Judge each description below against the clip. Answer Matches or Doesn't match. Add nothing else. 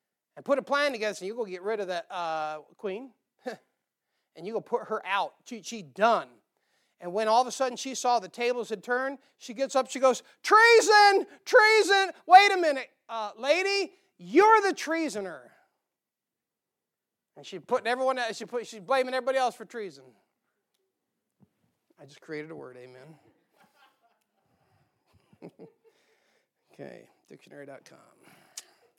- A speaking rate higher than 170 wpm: Doesn't match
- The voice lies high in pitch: Matches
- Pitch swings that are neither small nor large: Doesn't match